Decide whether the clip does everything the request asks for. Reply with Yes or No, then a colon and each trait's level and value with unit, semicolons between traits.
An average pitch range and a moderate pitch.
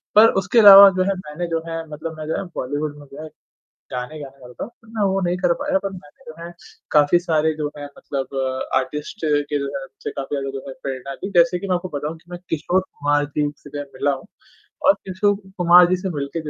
Yes: average, 4.0 semitones; medium, 155 Hz